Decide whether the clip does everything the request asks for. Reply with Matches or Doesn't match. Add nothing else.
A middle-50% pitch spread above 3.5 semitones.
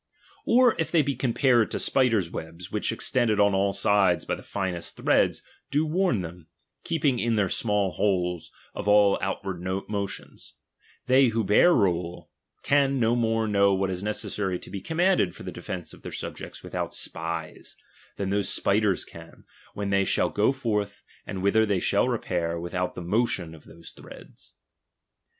Matches